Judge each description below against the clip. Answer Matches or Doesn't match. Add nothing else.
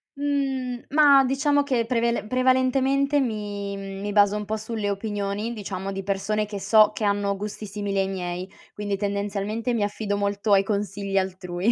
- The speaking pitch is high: Matches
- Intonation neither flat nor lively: Matches